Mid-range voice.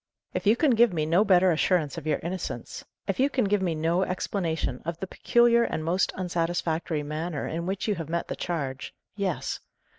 Yes: medium, 175 Hz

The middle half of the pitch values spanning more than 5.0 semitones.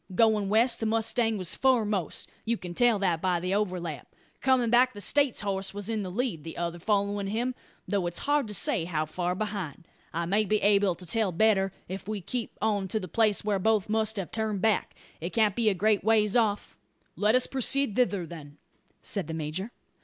No: average, 3.4 semitones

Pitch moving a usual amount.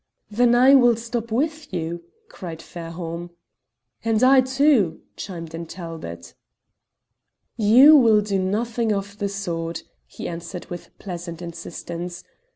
No: wide, 5.7 semitones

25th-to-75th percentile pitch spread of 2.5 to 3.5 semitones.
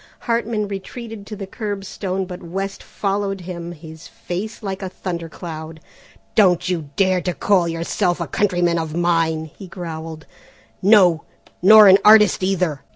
Yes: average, 2.9 semitones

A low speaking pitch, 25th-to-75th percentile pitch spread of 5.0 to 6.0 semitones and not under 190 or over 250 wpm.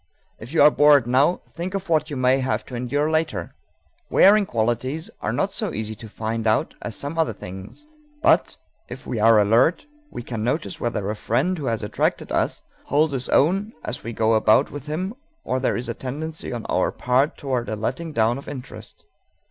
Yes: low, 130 Hz; wide, 5.4 semitones; average, 200 wpm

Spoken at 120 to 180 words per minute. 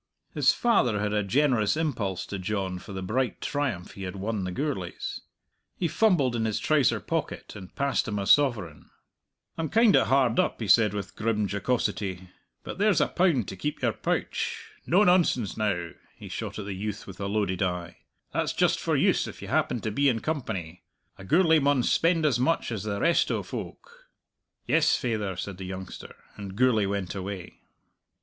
No: average, 190 wpm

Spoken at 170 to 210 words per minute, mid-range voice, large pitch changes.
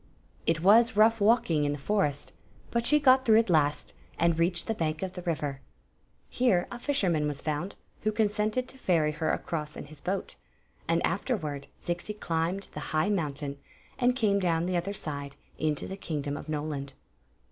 Yes: average, 180 wpm; medium, 175 Hz; wide, 5.8 semitones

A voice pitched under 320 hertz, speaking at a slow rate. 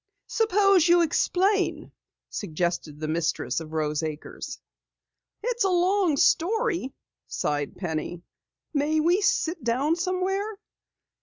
No: very high, 330 Hz; slow, 105 wpm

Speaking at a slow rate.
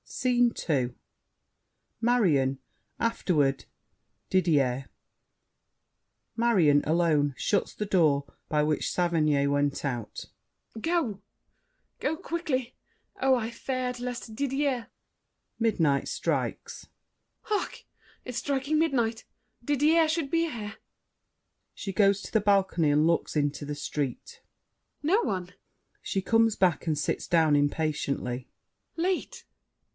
Yes: slow, 105 wpm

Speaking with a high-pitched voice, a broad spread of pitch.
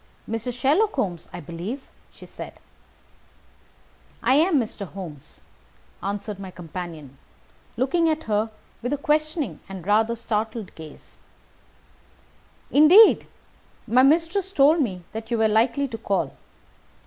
Yes: high, 225 Hz; wide, 7.0 semitones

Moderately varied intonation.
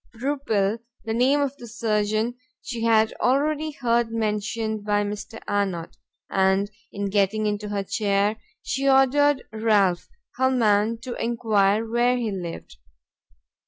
Yes: average, 3.1 semitones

